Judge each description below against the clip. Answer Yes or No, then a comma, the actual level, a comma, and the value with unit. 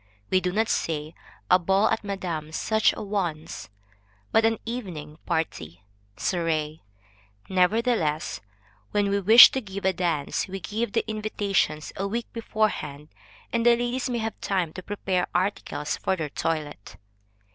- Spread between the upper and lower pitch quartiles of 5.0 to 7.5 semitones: Yes, average, 5.3 semitones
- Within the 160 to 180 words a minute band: No, average, 145 wpm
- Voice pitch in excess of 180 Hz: Yes, high, 190 Hz